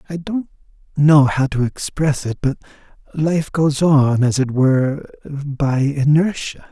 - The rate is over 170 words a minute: No, average, 145 wpm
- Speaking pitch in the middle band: Yes, medium, 145 Hz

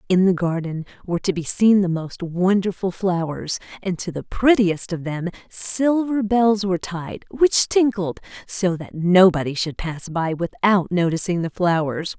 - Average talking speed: Yes, average, 165 wpm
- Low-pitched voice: No, medium, 185 Hz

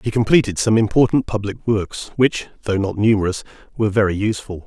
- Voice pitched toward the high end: No, low, 105 Hz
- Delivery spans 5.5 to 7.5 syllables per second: Yes, 6.0 syllables/s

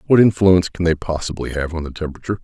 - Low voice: Yes, very low, 85 Hz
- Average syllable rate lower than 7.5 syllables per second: No, 7.6 syllables/s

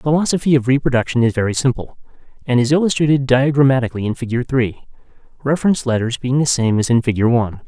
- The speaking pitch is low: Yes, low, 130 Hz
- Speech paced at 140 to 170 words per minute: No, average, 180 wpm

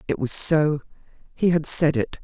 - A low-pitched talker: No, medium, 150 Hz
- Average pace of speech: Yes, average, 190 wpm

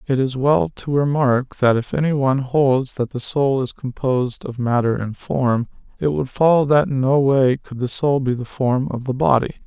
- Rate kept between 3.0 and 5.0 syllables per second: Yes, 4.6 syllables/s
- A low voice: Yes, low, 130 Hz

